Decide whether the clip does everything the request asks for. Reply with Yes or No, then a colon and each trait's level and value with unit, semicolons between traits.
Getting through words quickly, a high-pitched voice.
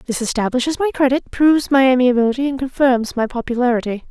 No: average, 160 wpm; very high, 255 Hz